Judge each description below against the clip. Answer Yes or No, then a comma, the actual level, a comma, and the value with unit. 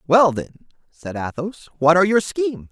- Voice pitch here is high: No, medium, 175 Hz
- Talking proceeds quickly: No, average, 175 wpm